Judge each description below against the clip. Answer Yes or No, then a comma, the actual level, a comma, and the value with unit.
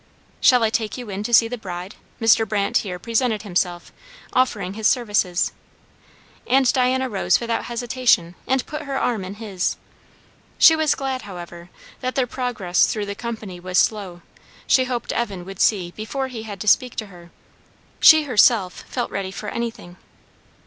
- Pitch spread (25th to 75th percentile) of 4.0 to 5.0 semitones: Yes, average, 4.7 semitones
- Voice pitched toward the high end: Yes, high, 220 Hz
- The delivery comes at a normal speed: Yes, average, 170 wpm